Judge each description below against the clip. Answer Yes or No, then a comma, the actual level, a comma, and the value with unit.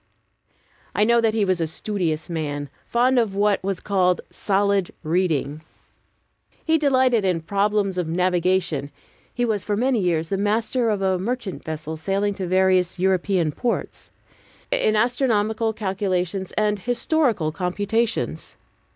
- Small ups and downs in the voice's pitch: No, average, 3.6 semitones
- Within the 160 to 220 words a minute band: No, slow, 135 wpm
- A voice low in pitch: No, high, 195 Hz